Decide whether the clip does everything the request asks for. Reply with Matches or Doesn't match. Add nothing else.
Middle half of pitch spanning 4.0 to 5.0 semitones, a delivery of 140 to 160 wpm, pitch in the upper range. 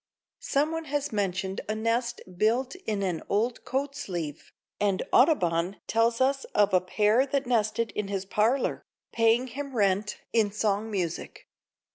Matches